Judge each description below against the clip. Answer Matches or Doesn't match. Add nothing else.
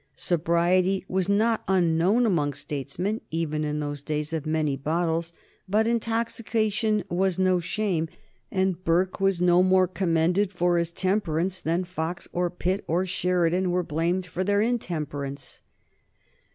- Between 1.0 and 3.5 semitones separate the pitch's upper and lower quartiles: Matches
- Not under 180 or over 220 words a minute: Doesn't match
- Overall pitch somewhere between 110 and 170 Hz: Doesn't match